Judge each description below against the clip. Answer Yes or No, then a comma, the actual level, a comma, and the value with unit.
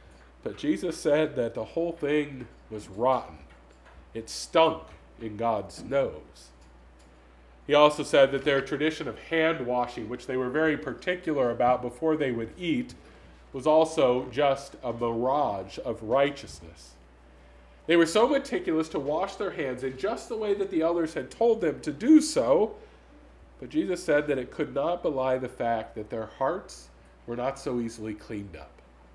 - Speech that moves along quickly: No, average, 165 wpm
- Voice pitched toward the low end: Yes, low, 130 Hz